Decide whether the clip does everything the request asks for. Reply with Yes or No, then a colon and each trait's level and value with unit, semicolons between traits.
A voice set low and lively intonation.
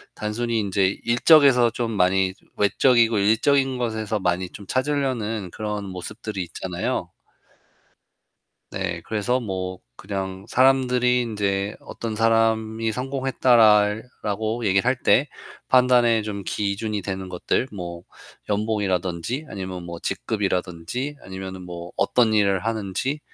No: low, 105 Hz; average, 3.9 semitones